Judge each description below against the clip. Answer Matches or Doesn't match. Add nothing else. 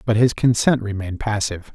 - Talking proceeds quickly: Doesn't match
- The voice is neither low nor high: Doesn't match